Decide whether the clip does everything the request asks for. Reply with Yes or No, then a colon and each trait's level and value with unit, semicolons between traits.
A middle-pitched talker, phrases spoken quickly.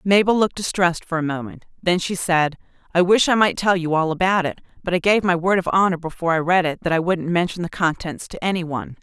Yes: medium, 175 Hz; fast, 255 wpm